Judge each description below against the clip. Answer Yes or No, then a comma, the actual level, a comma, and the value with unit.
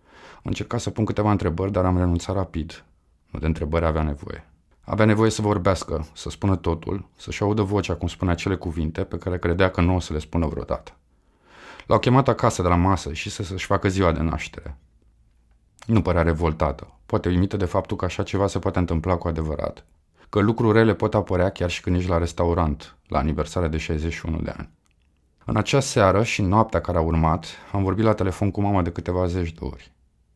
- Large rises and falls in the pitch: No, average, 3.6 semitones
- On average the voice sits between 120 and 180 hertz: No, very low, 90 Hz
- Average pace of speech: No, fast, 200 wpm